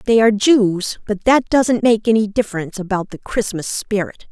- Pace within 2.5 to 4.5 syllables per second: No, 5.1 syllables/s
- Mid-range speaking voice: No, high, 215 Hz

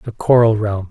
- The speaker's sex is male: Yes, male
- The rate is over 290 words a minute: No, average, 200 wpm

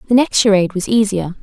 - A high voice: Yes, high, 210 Hz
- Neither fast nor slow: No, fast, 210 wpm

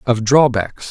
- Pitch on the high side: No, low, 120 Hz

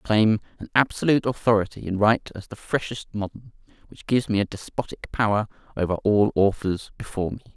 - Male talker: Yes, male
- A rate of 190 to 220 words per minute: No, average, 175 wpm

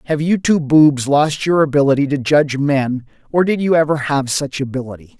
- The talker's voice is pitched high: No, medium, 145 Hz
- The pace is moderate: Yes, average, 195 wpm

